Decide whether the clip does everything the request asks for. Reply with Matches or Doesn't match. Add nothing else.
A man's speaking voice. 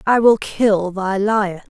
Doesn't match